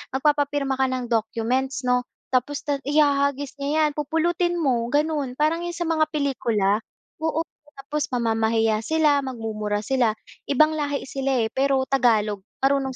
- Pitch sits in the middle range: No, very high, 270 Hz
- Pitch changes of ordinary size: Yes, average, 3.7 semitones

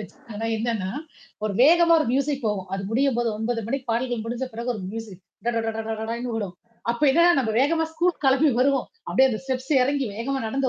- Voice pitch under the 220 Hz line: No, high, 245 Hz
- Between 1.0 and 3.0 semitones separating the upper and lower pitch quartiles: No, average, 3.6 semitones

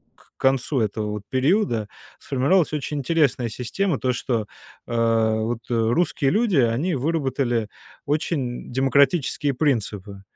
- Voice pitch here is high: No, low, 130 Hz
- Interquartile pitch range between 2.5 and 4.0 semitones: No, average, 4.4 semitones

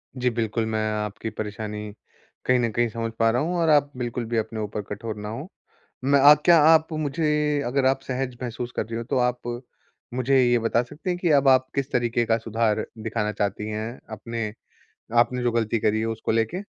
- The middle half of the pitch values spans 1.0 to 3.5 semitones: Yes, average, 3.1 semitones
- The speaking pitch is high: No, low, 120 Hz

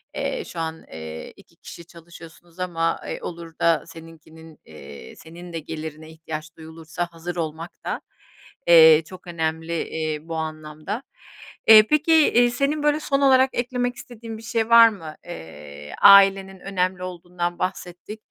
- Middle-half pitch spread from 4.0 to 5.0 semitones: Yes, average, 4.7 semitones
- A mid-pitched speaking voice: Yes, medium, 170 Hz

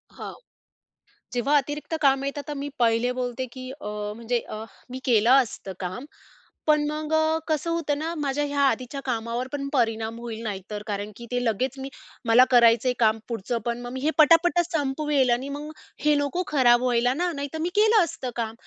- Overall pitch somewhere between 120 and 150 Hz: No, very high, 255 Hz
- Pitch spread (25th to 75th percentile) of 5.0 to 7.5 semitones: No, average, 3.8 semitones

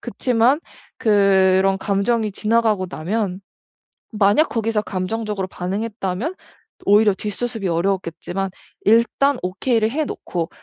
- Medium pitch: No, high, 210 Hz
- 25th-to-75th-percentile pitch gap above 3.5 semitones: No, average, 3.2 semitones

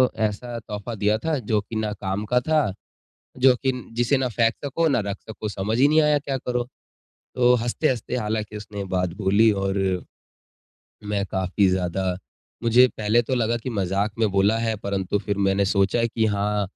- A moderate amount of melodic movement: Yes, average, 3.5 semitones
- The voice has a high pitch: No, low, 110 Hz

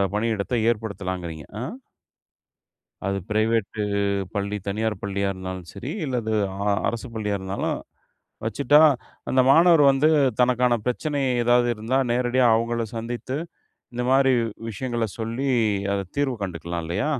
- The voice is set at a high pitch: No, low, 115 Hz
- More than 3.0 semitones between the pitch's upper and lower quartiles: Yes, average, 4.0 semitones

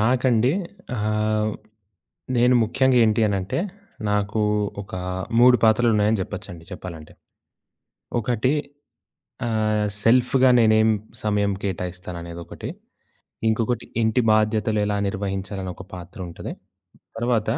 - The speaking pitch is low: Yes, low, 110 Hz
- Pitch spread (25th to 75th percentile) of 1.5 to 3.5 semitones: Yes, average, 2.8 semitones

